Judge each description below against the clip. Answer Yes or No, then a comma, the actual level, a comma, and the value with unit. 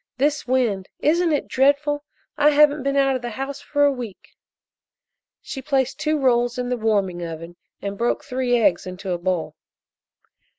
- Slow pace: No, average, 170 wpm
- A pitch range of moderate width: No, wide, 6.0 semitones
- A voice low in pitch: No, very high, 255 Hz